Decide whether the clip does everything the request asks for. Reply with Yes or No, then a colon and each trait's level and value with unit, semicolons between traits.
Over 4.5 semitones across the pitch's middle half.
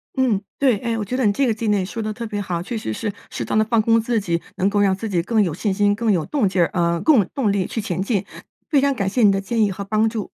No: average, 2.9 semitones